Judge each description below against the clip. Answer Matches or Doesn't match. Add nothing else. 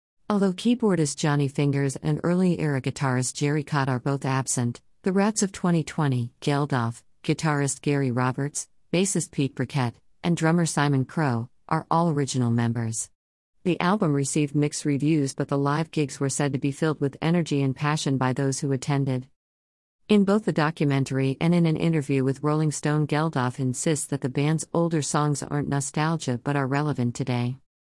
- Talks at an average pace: Matches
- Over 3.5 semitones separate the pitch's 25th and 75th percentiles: Doesn't match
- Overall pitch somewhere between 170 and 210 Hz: Doesn't match